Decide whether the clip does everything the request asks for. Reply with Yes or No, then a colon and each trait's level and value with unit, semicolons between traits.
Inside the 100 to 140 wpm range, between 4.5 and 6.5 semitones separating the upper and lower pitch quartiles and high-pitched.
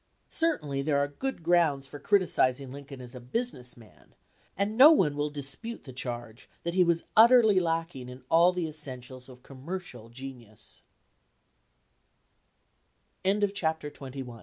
No: slow, 135 wpm; wide, 5.5 semitones; medium, 145 Hz